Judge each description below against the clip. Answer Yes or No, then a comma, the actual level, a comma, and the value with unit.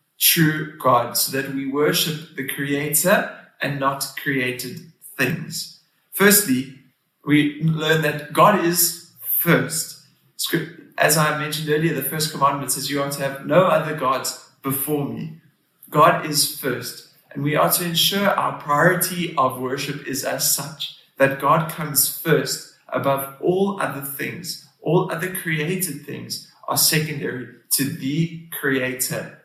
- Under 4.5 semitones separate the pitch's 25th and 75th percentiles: Yes, average, 3.2 semitones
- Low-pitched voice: No, medium, 150 Hz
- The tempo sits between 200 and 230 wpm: No, average, 140 wpm